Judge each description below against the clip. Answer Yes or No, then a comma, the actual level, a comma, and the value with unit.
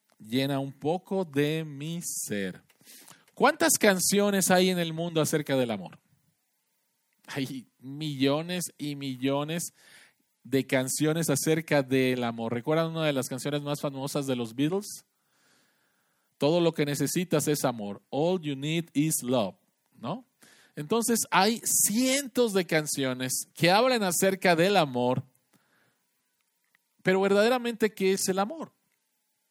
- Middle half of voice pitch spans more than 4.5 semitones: Yes, wide, 5.5 semitones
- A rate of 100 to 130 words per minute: Yes, slow, 125 wpm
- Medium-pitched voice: Yes, medium, 155 Hz